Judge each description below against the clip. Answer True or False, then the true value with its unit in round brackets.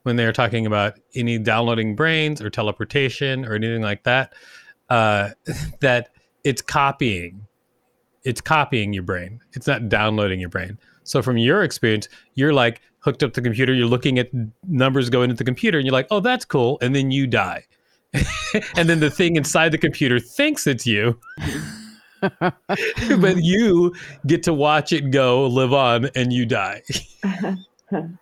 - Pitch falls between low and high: False (130 Hz)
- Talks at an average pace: True (165 wpm)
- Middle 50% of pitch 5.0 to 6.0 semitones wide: True (5.3 semitones)